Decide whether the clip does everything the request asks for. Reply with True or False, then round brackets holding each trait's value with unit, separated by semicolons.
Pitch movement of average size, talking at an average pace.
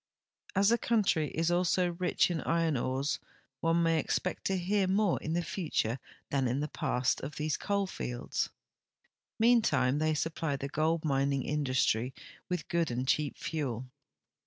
True (4.4 semitones; 160 wpm)